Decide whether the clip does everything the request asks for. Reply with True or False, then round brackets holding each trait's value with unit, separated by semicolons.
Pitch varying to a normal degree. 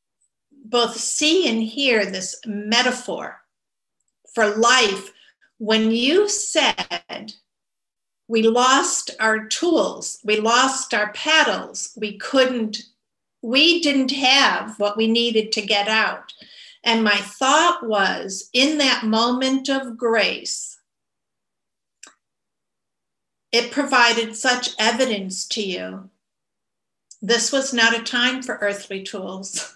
True (3.5 semitones)